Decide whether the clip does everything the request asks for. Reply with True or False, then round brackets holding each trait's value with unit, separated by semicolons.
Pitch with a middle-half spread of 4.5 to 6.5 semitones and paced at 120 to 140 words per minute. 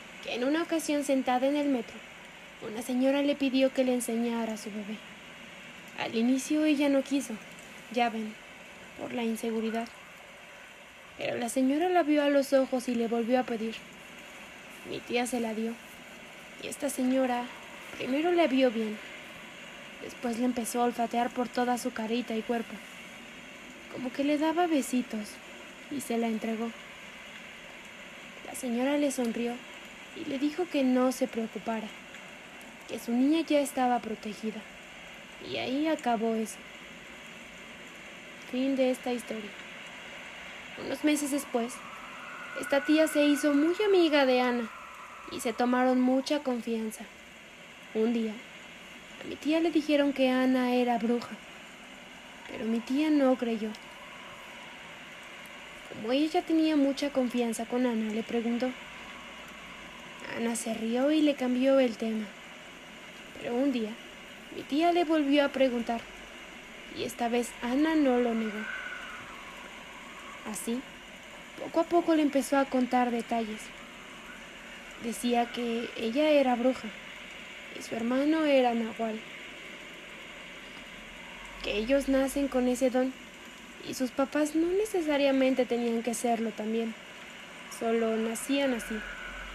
False (3.4 semitones; 135 wpm)